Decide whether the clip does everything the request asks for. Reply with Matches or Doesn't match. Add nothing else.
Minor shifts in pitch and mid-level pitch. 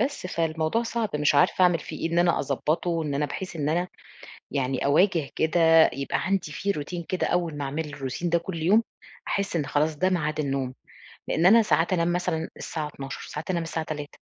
Doesn't match